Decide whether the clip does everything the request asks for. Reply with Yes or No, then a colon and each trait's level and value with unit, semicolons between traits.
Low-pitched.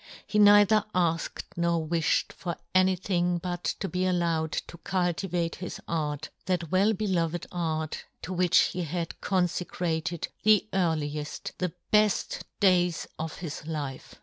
No: medium, 175 Hz